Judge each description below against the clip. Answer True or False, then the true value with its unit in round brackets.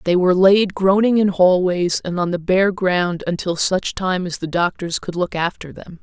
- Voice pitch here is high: False (180 Hz)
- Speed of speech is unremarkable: False (210 wpm)